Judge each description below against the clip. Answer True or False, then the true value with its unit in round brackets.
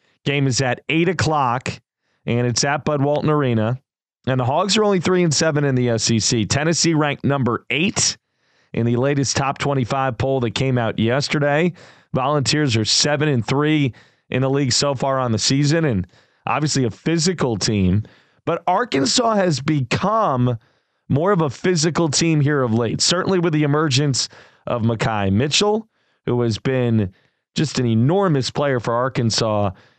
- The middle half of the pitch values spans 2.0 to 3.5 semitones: False (4.2 semitones)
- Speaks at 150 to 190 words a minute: True (165 wpm)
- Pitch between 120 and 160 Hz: True (140 Hz)